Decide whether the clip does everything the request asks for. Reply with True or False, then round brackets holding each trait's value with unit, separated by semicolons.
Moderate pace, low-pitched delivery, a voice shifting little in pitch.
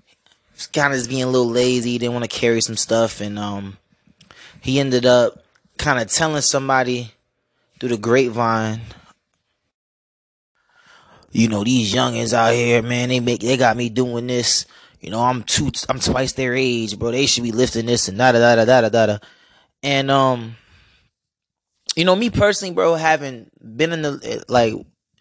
True (175 wpm; 120 Hz; 2.3 semitones)